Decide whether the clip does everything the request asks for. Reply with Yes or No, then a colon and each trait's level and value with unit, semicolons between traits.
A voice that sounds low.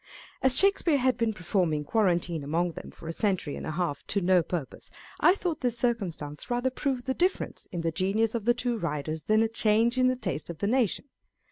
No: high, 210 Hz